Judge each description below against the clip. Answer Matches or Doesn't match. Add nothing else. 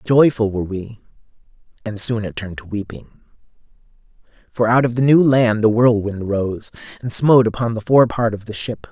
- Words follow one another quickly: Doesn't match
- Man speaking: Matches